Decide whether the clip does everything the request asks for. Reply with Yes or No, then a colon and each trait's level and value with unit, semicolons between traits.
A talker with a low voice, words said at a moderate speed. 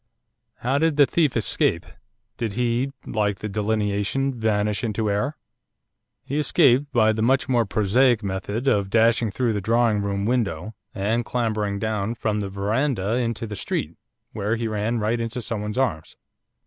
Yes: low, 110 Hz; average, 160 wpm